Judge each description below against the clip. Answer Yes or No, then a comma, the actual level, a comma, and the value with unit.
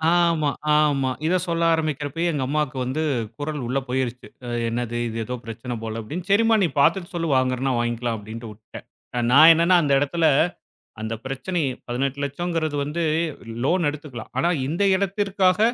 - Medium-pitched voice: Yes, medium, 145 Hz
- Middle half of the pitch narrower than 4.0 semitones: No, average, 5.1 semitones